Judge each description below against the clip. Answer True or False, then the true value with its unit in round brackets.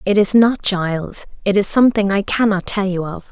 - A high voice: True (200 Hz)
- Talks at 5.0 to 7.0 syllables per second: True (5.4 syllables/s)